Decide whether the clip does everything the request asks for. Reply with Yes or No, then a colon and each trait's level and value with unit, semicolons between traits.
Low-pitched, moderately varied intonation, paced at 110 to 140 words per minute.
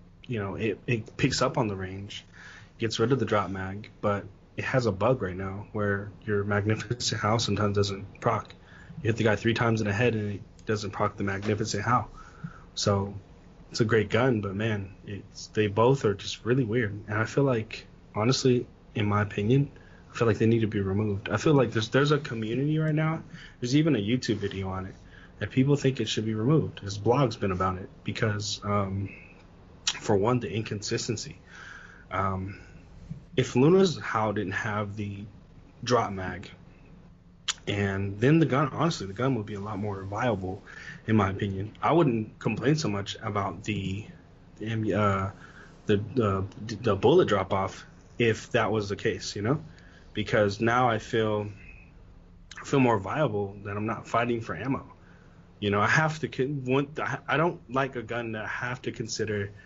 No: low, 105 Hz; average, 3.6 semitones; average, 185 wpm